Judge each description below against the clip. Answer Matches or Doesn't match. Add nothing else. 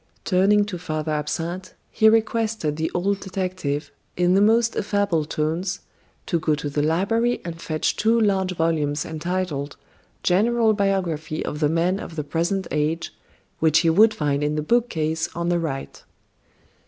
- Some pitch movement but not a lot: Matches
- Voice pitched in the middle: Matches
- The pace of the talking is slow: Doesn't match